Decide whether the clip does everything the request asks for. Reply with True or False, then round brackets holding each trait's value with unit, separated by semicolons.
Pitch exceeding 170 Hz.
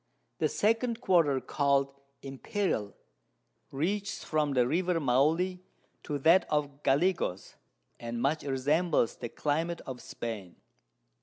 False (145 Hz)